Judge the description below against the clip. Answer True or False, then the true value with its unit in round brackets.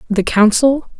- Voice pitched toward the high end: True (230 Hz)